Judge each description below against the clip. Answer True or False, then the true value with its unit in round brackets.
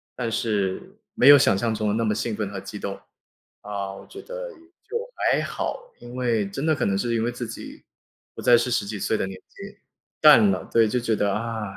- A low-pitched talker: True (115 Hz)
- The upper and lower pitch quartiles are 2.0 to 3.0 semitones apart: False (3.4 semitones)